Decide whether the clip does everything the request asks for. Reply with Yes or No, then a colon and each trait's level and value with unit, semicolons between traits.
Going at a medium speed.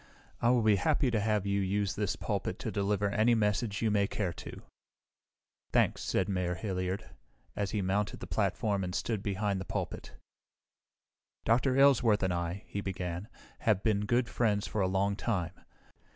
Yes: average, 170 wpm